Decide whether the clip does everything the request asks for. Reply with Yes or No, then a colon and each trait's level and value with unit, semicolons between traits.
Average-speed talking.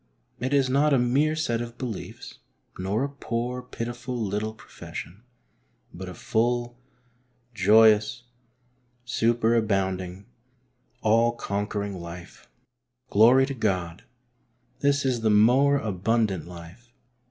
No: slow, 115 wpm